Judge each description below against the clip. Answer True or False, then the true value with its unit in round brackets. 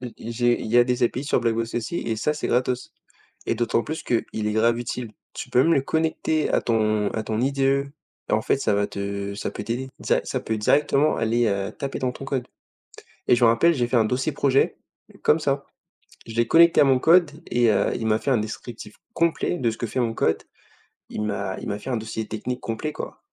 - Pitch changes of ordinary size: True (3.6 semitones)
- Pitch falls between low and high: False (120 Hz)